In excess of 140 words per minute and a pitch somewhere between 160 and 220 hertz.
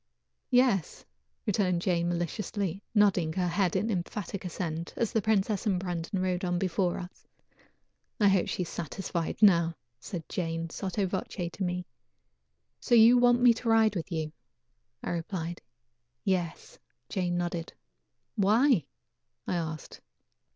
No: slow, 135 wpm; medium, 185 Hz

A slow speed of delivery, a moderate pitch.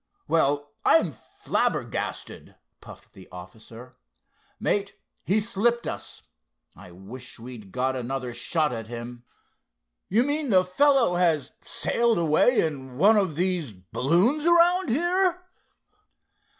Yes: slow, 115 wpm; medium, 165 Hz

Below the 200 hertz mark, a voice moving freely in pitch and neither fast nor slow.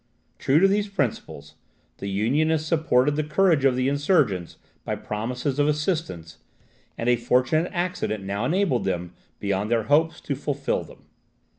Yes: medium, 140 Hz; wide, 6.5 semitones; average, 150 wpm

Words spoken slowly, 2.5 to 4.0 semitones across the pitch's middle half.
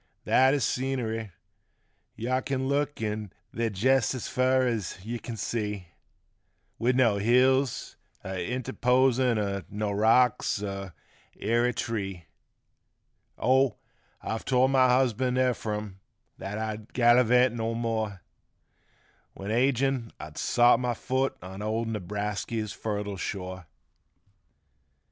Yes: slow, 115 wpm; average, 3.6 semitones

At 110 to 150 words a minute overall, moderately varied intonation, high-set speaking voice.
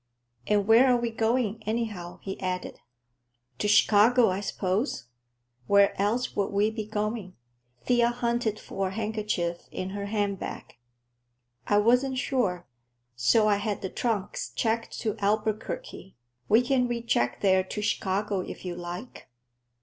Yes: average, 140 wpm; average, 3.0 semitones; high, 210 Hz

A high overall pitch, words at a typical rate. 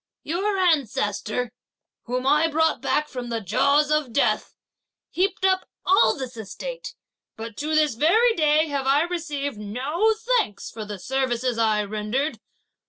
Yes: very high, 280 Hz; average, 150 wpm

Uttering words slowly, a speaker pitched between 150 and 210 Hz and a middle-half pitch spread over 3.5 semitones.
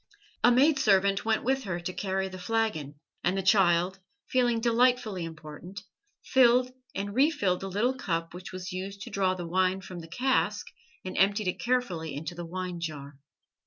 No: average, 175 wpm; high, 190 Hz; average, 4.6 semitones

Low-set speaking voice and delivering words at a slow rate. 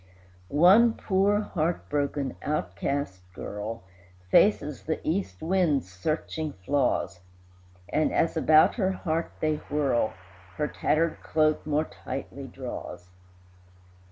No: medium, 155 Hz; slow, 105 wpm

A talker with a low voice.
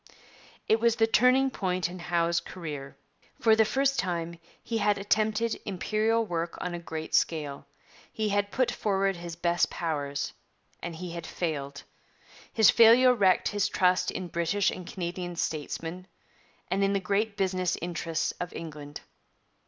No: medium, 180 Hz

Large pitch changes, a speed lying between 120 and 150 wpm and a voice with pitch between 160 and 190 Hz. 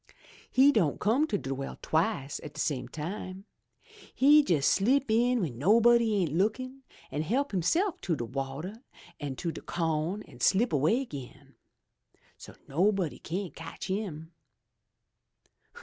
Yes: wide, 7.2 semitones; average, 140 wpm; medium, 185 Hz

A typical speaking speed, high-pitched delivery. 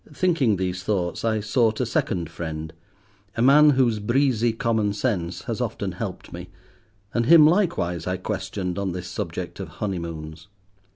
No: average, 150 wpm; low, 100 Hz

